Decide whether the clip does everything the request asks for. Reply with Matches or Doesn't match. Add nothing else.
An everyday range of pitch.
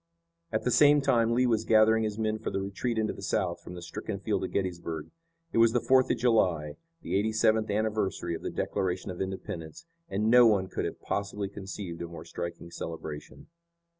Matches